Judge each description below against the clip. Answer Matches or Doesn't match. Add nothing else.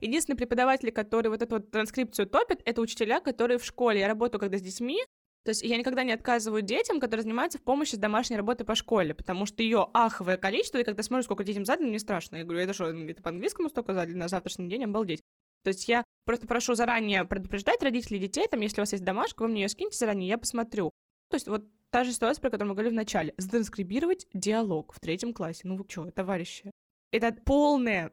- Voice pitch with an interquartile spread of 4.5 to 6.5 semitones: Doesn't match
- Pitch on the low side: Doesn't match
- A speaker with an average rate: Doesn't match